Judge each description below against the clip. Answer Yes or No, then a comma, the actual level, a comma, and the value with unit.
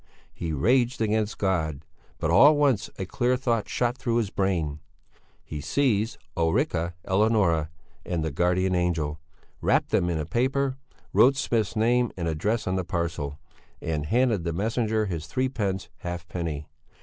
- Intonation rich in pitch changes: Yes, wide, 6.1 semitones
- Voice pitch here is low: Yes, very low, 95 Hz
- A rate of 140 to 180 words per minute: Yes, average, 150 wpm